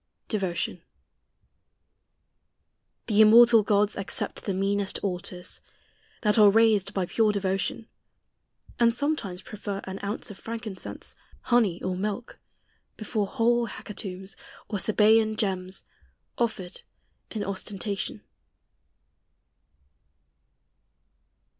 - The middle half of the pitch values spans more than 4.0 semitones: No, narrow, 2.6 semitones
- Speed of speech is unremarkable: No, slow, 90 wpm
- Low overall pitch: No, high, 205 Hz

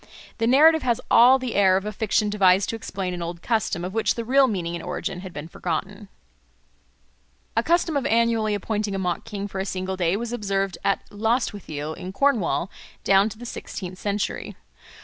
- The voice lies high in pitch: Yes, high, 205 Hz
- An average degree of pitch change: Yes, average, 3.5 semitones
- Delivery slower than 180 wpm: No, average, 190 wpm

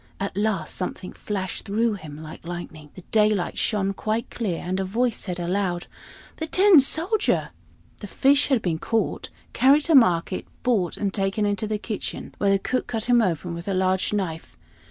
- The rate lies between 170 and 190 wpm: Yes, average, 180 wpm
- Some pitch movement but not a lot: Yes, average, 4.1 semitones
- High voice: Yes, high, 200 Hz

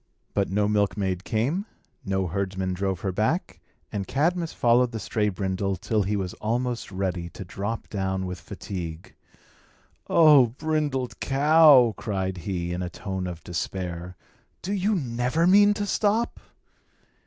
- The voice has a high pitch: No, low, 105 Hz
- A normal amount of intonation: No, wide, 6.2 semitones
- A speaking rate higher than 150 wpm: No, average, 140 wpm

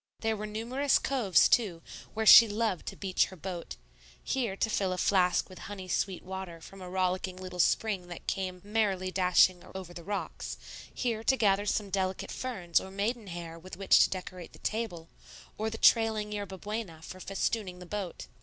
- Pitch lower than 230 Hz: Yes, high, 190 Hz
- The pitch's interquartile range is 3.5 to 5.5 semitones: No, average, 2.9 semitones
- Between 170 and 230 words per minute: Yes, average, 185 wpm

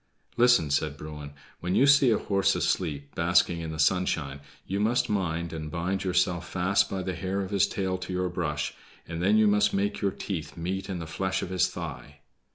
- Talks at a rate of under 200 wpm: No, fast, 205 wpm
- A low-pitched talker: Yes, very low, 90 Hz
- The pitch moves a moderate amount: Yes, average, 3.3 semitones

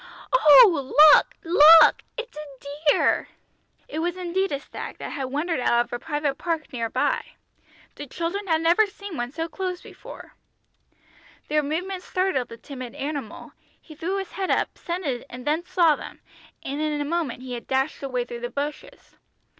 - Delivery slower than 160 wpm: No, average, 170 wpm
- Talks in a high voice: Yes, very high, 305 Hz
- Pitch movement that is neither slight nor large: Yes, average, 4.5 semitones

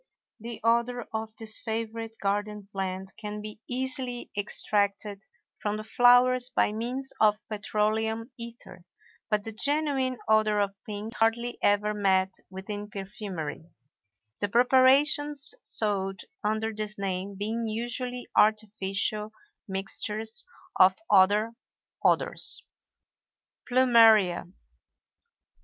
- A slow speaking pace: Yes, slow, 110 wpm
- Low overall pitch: No, high, 215 Hz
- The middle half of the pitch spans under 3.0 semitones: Yes, narrow, 2.5 semitones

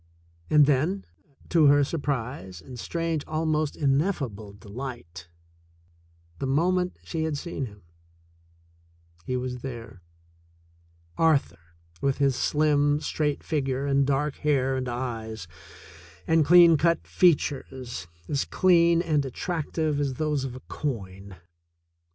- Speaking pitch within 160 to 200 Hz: No, medium, 140 Hz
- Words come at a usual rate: No, slow, 125 wpm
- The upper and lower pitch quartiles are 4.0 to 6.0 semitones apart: Yes, average, 4.4 semitones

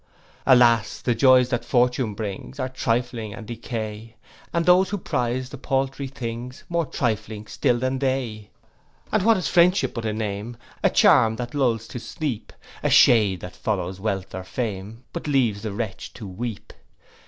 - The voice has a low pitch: Yes, low, 120 Hz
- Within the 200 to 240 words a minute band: No, average, 165 wpm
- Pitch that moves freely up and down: No, average, 3.4 semitones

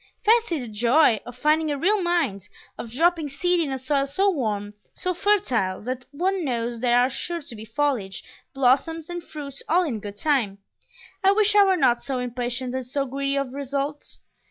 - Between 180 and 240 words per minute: Yes, average, 190 wpm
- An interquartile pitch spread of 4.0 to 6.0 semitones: Yes, wide, 5.4 semitones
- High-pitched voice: Yes, very high, 275 Hz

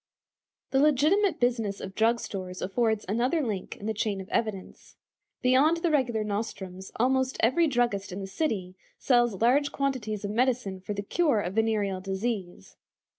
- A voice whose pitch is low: No, high, 225 Hz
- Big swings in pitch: No, average, 4.6 semitones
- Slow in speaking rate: No, average, 160 wpm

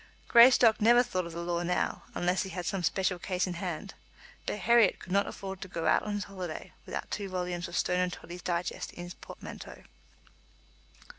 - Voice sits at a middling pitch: Yes, medium, 180 Hz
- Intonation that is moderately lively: No, narrow, 2.1 semitones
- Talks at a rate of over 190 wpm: Yes, average, 200 wpm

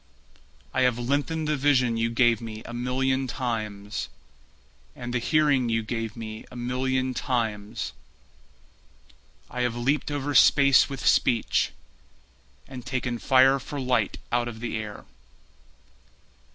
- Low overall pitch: Yes, low, 125 Hz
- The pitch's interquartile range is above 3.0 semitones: No, narrow, 2.4 semitones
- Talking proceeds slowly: Yes, slow, 130 wpm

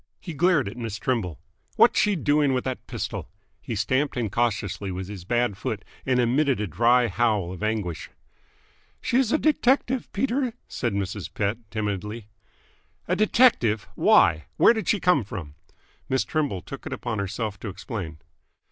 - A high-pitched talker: No, low, 115 Hz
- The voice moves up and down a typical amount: No, wide, 6.7 semitones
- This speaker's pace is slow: No, average, 160 wpm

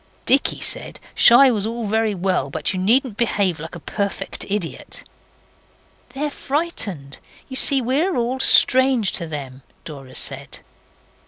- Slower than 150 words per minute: Yes, average, 140 wpm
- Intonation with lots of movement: Yes, wide, 7.2 semitones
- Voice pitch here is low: No, high, 215 Hz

